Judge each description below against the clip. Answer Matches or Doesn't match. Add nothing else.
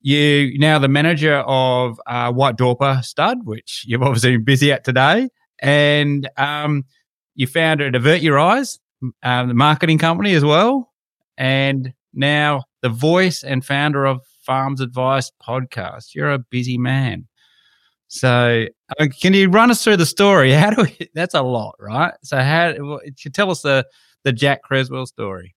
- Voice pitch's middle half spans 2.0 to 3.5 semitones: Matches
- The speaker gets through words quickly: Doesn't match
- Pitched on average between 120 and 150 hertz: Matches